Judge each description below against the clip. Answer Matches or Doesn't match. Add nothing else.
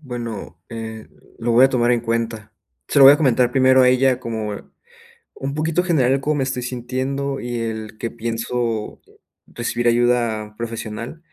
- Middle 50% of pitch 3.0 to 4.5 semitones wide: Doesn't match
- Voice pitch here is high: Doesn't match